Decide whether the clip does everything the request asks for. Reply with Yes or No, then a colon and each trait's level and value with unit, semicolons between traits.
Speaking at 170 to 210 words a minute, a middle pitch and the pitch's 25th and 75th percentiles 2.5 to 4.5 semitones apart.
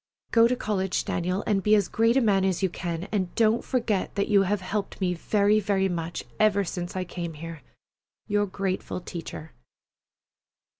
No: average, 180 wpm; high, 195 Hz; average, 2.9 semitones